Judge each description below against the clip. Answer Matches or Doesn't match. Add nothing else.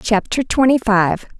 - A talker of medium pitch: Doesn't match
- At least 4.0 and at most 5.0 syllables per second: Matches